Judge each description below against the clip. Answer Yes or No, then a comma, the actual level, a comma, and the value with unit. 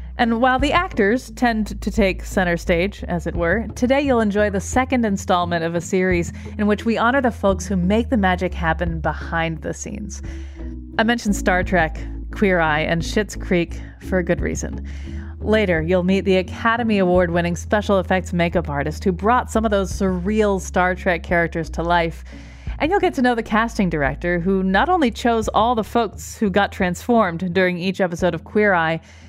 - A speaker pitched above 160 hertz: Yes, high, 190 Hz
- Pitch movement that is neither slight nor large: Yes, average, 4.3 semitones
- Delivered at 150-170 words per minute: No, average, 195 wpm